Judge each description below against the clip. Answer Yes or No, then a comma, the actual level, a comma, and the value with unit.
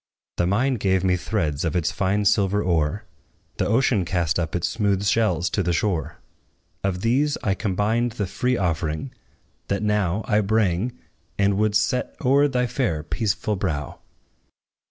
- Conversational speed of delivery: Yes, average, 155 wpm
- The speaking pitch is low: Yes, low, 100 Hz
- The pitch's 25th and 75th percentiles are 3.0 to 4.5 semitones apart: Yes, average, 4.0 semitones